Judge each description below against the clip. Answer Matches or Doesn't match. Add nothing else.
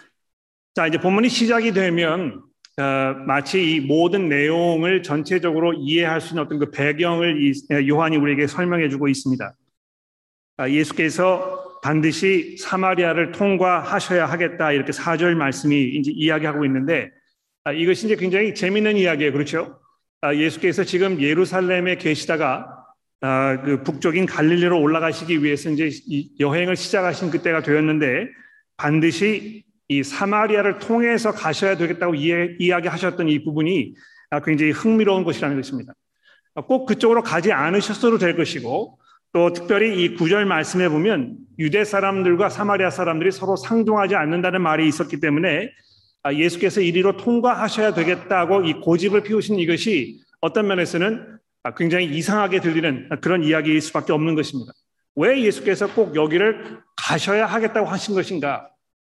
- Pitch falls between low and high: Matches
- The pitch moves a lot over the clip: Doesn't match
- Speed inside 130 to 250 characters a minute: Doesn't match